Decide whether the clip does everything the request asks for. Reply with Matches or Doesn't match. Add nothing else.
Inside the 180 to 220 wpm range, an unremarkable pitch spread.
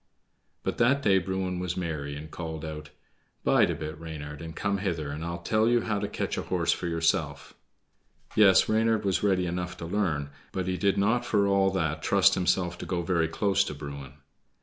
Matches